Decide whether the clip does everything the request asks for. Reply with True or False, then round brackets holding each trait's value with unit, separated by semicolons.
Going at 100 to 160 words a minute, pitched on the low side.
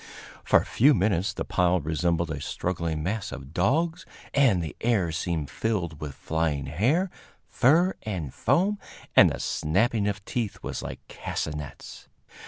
True (150 wpm; 90 Hz)